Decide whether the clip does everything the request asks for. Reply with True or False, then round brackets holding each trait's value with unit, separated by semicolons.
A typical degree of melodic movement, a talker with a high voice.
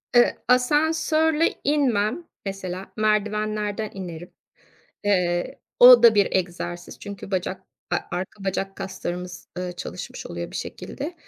True (4.7 semitones; 200 Hz)